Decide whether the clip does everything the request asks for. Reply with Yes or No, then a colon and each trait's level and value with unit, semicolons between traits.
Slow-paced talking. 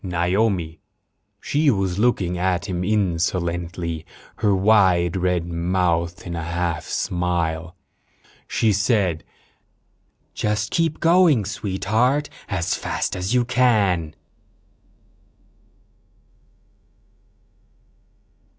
Yes: slow, 85 wpm